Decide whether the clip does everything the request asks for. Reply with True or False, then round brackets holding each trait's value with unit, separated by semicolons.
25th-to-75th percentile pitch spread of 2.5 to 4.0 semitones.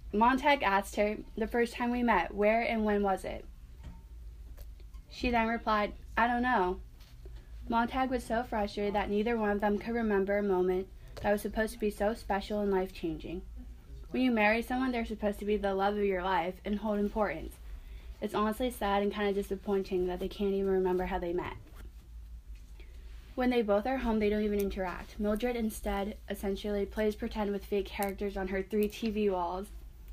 True (2.8 semitones)